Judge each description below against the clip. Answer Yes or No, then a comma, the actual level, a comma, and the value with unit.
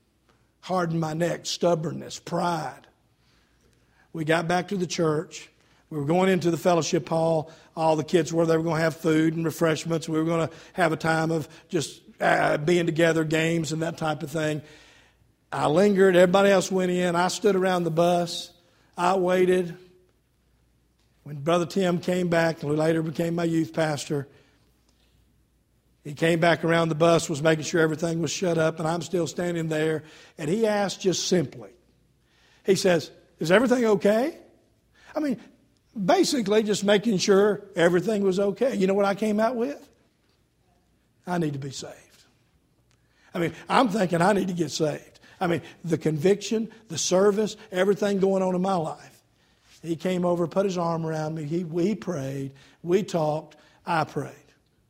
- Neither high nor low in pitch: Yes, medium, 170 Hz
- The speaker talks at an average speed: Yes, average, 175 wpm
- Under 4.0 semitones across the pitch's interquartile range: Yes, average, 2.7 semitones